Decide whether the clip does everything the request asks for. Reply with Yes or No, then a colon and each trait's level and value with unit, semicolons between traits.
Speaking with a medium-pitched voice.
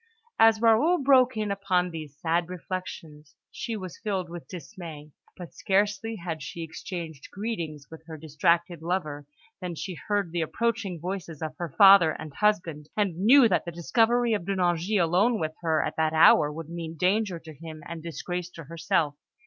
Yes: medium, 175 Hz